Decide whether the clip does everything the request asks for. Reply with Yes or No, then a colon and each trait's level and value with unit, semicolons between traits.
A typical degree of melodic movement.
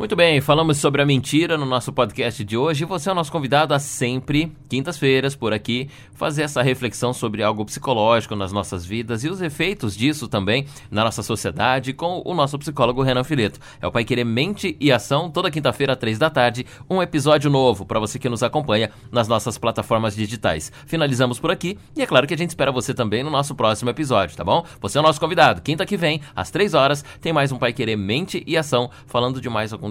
Yes: average, 4.6 semitones